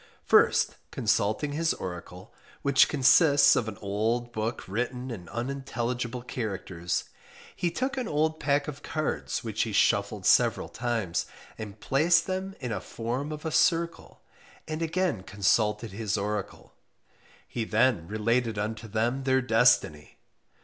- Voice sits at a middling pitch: No, low, 120 Hz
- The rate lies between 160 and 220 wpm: No, slow, 135 wpm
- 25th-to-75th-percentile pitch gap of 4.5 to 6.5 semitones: Yes, average, 5.2 semitones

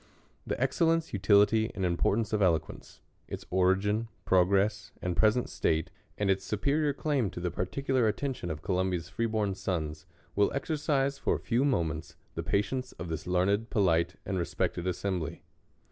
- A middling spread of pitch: Yes, average, 4.5 semitones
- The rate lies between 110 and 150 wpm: No, average, 160 wpm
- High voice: No, low, 100 Hz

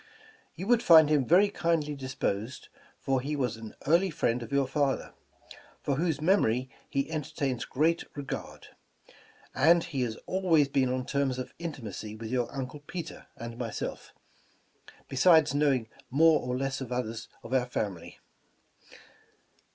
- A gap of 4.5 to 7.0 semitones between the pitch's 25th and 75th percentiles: No, average, 4.0 semitones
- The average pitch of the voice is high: No, low, 135 Hz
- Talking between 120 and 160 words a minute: Yes, average, 145 wpm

